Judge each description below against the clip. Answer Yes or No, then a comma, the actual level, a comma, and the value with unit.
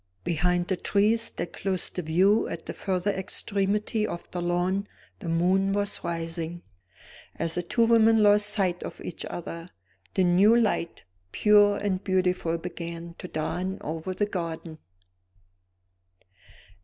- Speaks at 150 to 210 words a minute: No, average, 140 wpm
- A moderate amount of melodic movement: Yes, average, 3.1 semitones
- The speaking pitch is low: No, medium, 185 Hz